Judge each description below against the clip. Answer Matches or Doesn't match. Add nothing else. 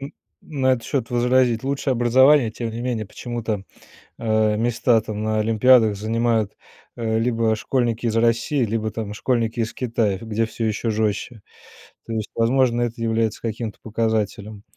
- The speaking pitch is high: Doesn't match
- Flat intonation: Matches